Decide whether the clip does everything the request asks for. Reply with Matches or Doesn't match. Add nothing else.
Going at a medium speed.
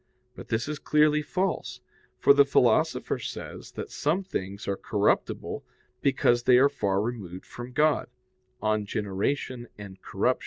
Matches